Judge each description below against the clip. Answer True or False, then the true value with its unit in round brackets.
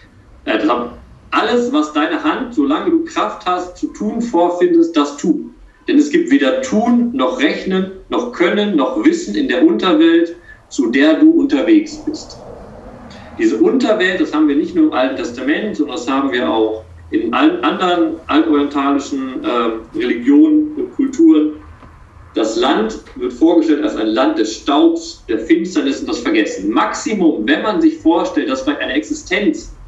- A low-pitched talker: False (310 Hz)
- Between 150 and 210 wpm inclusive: True (160 wpm)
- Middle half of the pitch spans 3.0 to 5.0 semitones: False (5.4 semitones)